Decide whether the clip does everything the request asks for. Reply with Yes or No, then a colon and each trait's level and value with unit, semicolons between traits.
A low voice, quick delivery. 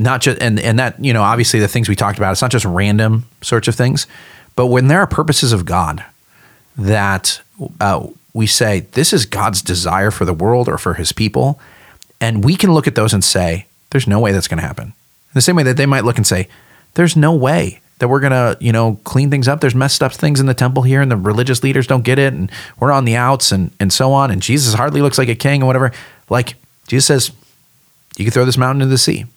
Yes: low, 125 Hz; fast, 250 wpm